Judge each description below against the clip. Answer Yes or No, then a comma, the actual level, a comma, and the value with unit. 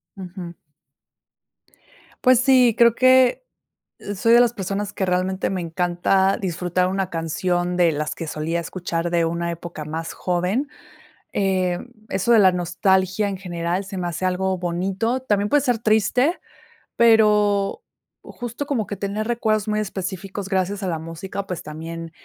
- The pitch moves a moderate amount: Yes, average, 3.4 semitones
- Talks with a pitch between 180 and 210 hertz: Yes, high, 190 Hz